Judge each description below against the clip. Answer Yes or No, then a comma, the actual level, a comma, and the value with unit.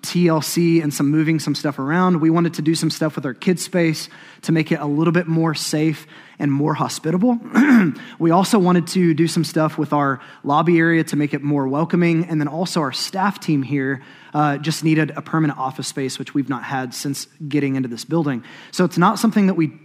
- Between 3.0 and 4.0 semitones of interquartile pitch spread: No, narrow, 2.6 semitones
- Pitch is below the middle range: No, medium, 160 Hz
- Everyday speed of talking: No, fast, 220 wpm